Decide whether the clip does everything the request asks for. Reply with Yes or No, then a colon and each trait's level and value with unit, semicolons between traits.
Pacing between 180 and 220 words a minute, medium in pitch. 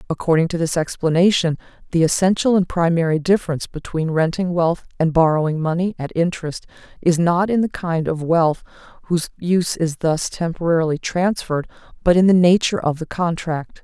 No: average, 160 wpm; medium, 170 Hz